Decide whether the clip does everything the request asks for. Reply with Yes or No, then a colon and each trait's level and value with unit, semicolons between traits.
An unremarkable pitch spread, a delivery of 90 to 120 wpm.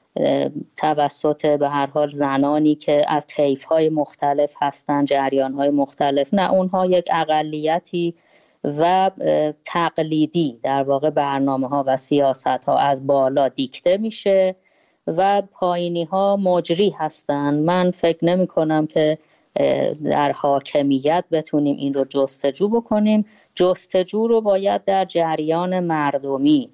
Yes: average, 4.3 semitones; average, 115 wpm